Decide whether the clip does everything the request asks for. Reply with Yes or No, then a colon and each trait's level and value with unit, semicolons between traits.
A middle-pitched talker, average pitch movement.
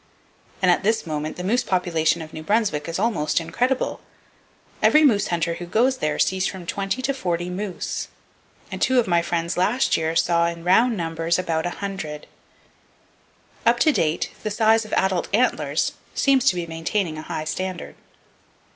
Yes: medium, 180 Hz; average, 4.8 semitones